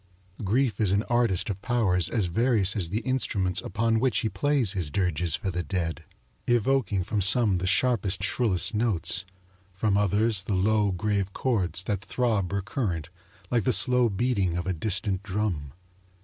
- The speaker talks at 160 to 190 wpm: Yes, average, 165 wpm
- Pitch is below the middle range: Yes, low, 100 Hz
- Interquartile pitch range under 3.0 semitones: No, average, 3.9 semitones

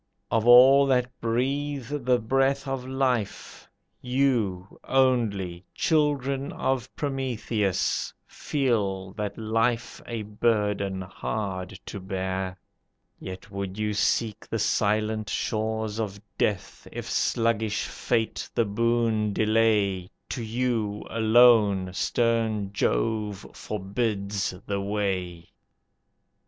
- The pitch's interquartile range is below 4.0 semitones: Yes, average, 3.6 semitones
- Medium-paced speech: No, slow, 100 wpm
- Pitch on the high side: No, low, 110 Hz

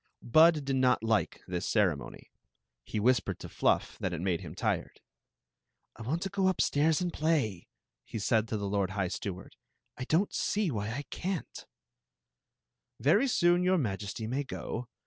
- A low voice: Yes, low, 125 Hz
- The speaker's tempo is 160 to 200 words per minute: Yes, average, 170 wpm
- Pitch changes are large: Yes, wide, 8.1 semitones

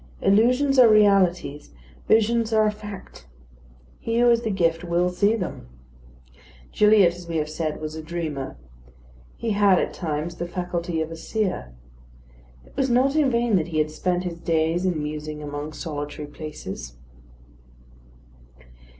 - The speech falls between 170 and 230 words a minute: No, average, 150 wpm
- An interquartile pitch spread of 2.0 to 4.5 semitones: No, wide, 5.5 semitones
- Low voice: No, medium, 175 Hz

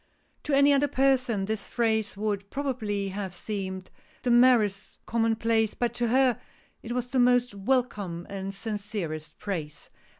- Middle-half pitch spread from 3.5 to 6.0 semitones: Yes, average, 3.9 semitones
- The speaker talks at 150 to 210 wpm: No, average, 140 wpm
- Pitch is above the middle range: Yes, high, 220 Hz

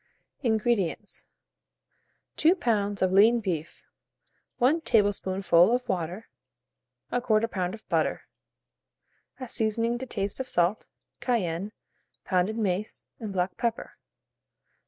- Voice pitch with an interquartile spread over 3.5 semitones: Yes, average, 3.9 semitones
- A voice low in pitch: No, high, 215 Hz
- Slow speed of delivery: Yes, slow, 105 wpm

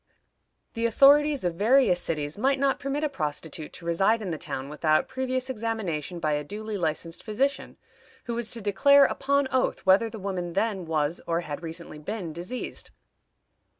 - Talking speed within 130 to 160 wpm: No, average, 170 wpm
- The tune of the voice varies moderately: No, wide, 7.4 semitones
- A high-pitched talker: Yes, high, 200 Hz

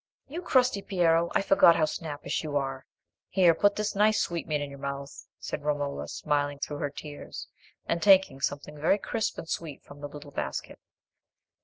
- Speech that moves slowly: No, average, 175 wpm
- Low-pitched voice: No, medium, 150 Hz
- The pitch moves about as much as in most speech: Yes, average, 5.0 semitones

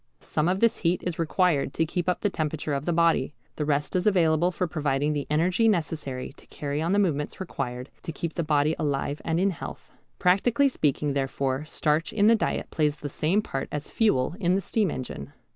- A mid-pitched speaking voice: Yes, medium, 160 Hz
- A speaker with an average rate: No, fast, 210 wpm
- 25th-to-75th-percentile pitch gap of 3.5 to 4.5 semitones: Yes, average, 3.8 semitones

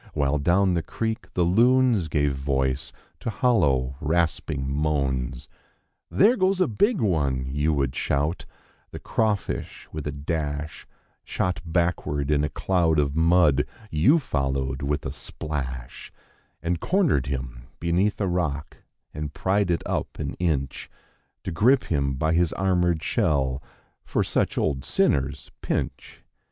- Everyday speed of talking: No, slow, 120 wpm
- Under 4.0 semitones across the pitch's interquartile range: No, average, 4.7 semitones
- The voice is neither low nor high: No, very low, 75 Hz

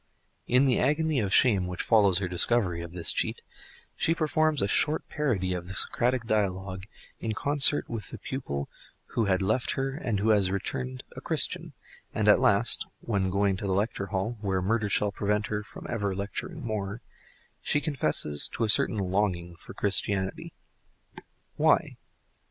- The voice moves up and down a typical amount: Yes, average, 4.1 semitones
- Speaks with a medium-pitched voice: No, low, 105 Hz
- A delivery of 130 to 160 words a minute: No, average, 170 wpm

